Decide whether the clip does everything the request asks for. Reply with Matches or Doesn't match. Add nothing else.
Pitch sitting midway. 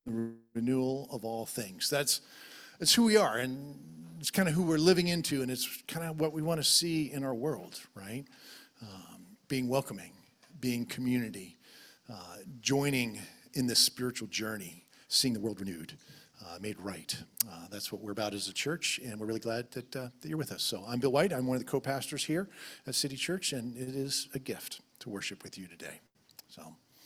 Doesn't match